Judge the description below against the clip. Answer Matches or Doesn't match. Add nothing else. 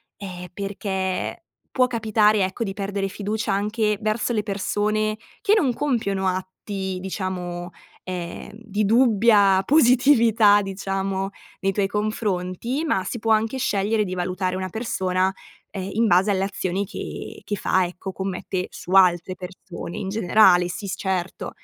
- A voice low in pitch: Doesn't match